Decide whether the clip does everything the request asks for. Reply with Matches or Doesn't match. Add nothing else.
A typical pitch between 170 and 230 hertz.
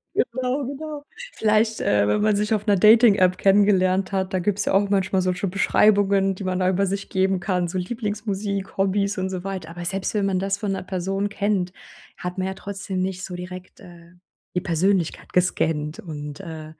Matches